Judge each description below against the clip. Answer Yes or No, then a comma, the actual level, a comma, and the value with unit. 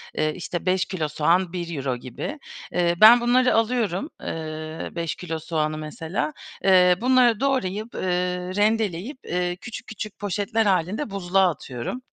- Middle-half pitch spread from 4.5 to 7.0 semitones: Yes, average, 5.3 semitones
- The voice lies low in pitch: No, medium, 185 Hz